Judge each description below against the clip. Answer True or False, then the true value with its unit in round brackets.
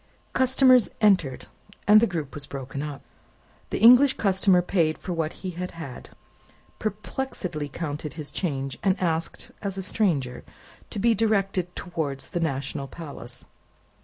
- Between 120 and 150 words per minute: True (140 wpm)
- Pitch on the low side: False (175 Hz)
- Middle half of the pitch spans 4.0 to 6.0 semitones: True (5.6 semitones)